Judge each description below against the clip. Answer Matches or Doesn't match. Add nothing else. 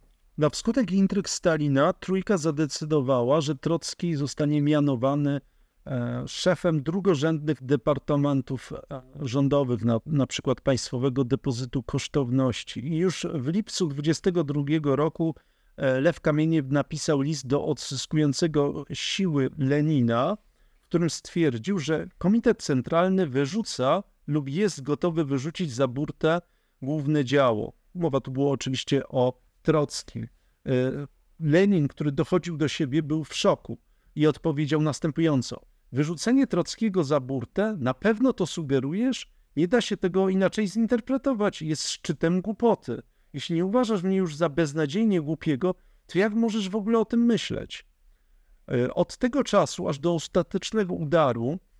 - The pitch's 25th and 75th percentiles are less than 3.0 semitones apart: Doesn't match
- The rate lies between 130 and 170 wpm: Doesn't match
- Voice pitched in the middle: Matches